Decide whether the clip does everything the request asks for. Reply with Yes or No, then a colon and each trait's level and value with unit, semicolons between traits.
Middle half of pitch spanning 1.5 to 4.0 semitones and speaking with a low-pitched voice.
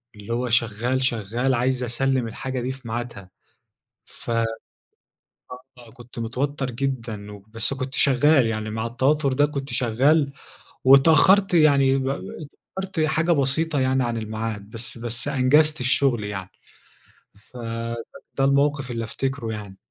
Yes: average, 3.3 semitones; low, 130 Hz